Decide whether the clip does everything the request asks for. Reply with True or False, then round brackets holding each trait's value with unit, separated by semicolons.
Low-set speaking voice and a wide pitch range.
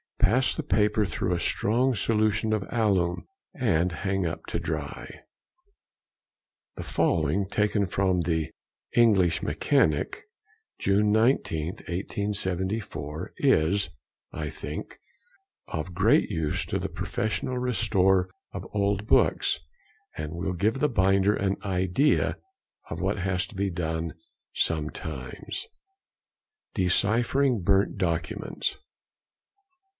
False (95 Hz; 3.8 semitones)